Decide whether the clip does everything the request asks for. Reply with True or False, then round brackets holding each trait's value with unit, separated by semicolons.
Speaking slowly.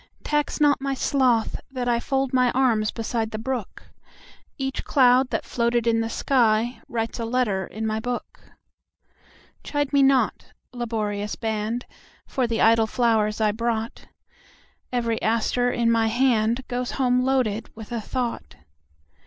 True (125 wpm)